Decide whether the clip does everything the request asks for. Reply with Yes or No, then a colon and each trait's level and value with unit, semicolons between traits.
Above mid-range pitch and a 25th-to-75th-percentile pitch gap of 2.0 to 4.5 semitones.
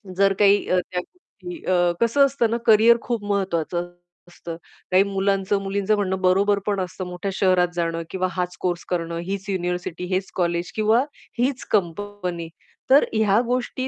Yes: high, 195 Hz; average, 2.9 semitones